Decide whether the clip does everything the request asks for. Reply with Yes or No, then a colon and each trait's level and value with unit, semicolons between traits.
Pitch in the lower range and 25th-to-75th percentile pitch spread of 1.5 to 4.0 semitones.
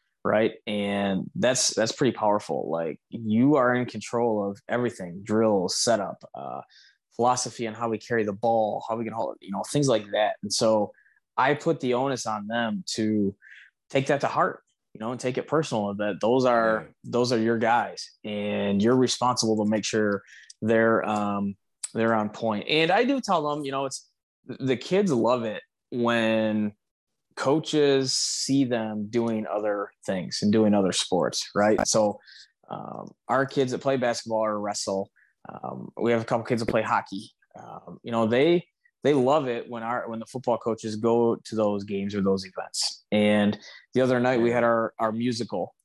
Yes: low, 115 Hz; average, 2.9 semitones